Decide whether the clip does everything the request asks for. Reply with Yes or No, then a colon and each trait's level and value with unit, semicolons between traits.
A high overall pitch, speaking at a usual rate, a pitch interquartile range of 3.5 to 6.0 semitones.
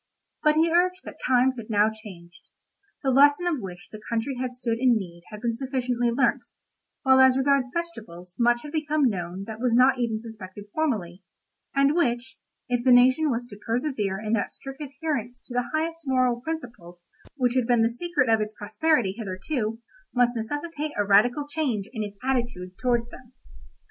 Yes: high, 245 Hz; average, 180 wpm; average, 4.2 semitones